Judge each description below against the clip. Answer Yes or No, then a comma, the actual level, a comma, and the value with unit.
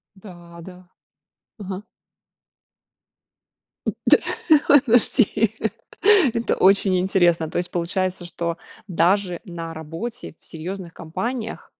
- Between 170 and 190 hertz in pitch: Yes, medium, 185 Hz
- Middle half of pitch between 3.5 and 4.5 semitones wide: No, average, 2.9 semitones